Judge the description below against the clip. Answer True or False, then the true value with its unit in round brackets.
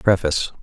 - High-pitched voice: False (90 Hz)